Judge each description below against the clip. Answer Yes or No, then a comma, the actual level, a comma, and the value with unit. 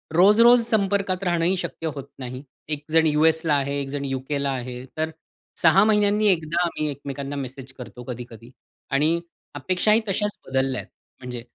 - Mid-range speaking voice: Yes, medium, 150 Hz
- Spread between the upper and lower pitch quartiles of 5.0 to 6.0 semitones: Yes, wide, 5.4 semitones